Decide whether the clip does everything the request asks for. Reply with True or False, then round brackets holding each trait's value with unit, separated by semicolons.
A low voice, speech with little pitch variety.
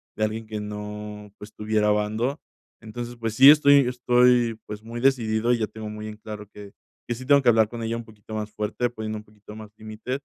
True (110 Hz; 2.2 semitones)